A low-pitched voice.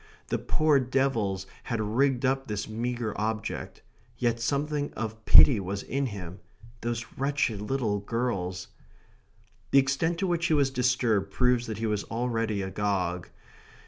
Yes: low, 115 Hz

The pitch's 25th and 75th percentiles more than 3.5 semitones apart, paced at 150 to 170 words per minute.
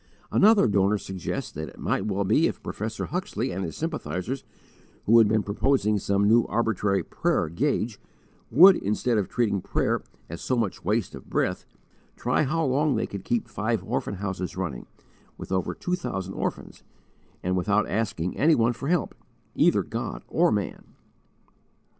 Yes: average, 4.8 semitones; average, 165 wpm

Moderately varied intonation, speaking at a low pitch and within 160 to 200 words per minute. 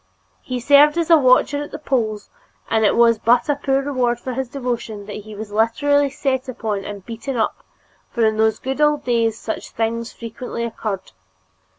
No: average, 3.7 semitones; high, 235 Hz; average, 190 wpm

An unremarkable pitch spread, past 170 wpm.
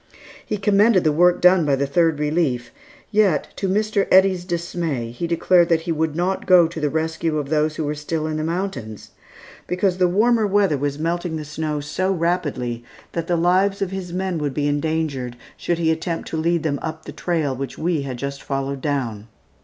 Yes: average, 3.5 semitones; average, 200 wpm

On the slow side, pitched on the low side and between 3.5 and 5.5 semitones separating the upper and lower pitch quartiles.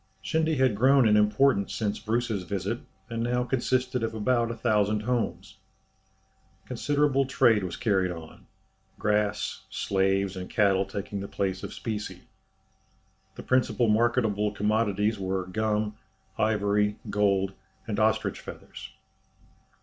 No: slow, 125 wpm; low, 105 Hz; average, 3.0 semitones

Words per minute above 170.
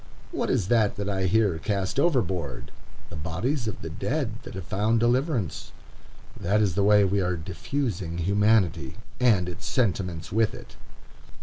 No: average, 160 wpm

